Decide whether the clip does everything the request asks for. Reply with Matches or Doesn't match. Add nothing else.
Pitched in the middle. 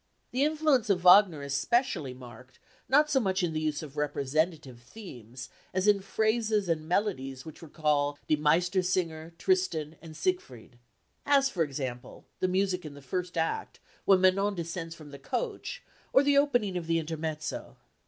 Matches